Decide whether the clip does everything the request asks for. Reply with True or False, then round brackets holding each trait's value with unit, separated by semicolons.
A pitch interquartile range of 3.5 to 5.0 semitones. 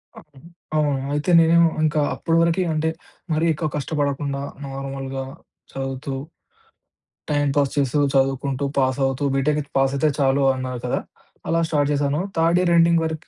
False (2.6 semitones)